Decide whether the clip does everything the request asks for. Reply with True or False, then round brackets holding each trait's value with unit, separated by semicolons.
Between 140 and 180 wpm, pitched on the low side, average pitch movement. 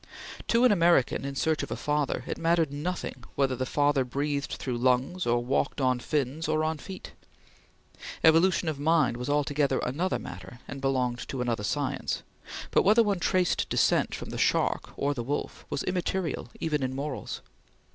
False (175 wpm; 145 Hz; 4.0 semitones)